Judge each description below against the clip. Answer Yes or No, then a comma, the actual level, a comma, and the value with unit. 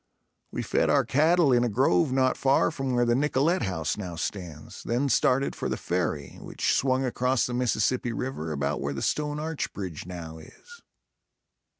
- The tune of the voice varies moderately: No, wide, 7.3 semitones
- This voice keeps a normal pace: Yes, average, 180 wpm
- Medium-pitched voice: No, low, 125 Hz